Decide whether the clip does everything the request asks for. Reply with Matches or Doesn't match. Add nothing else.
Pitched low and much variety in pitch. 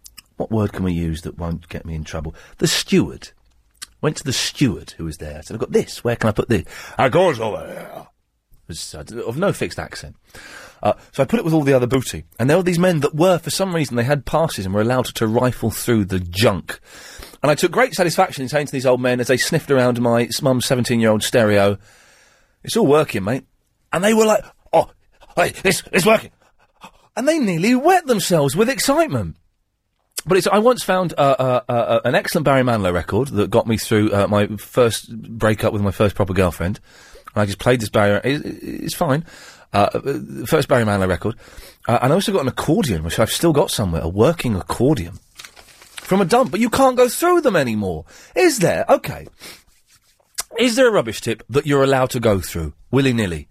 Matches